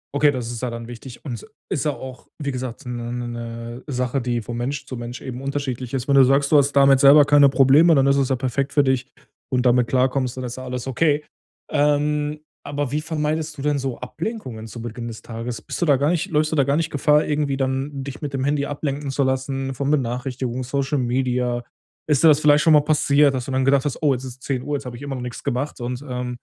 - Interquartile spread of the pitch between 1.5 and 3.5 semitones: Yes, narrow, 2.6 semitones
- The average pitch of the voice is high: No, low, 135 Hz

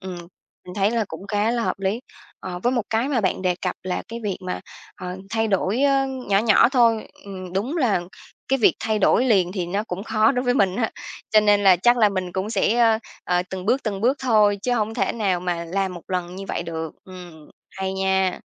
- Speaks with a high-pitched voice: Yes, high, 200 Hz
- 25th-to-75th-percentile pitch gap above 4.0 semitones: No, average, 3.7 semitones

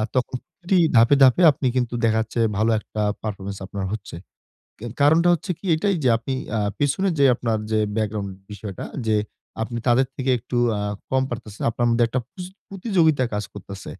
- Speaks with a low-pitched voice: Yes, low, 120 Hz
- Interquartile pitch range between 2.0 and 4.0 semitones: No, average, 4.8 semitones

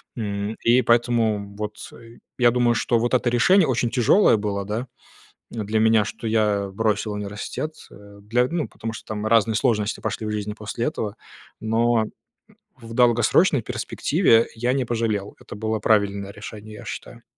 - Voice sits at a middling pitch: No, low, 110 Hz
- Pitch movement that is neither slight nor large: No, narrow, 2.2 semitones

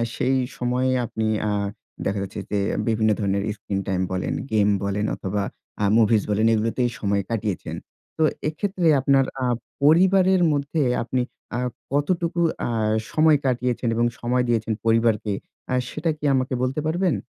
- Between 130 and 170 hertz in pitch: No, low, 120 Hz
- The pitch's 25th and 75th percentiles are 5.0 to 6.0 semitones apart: Yes, wide, 5.6 semitones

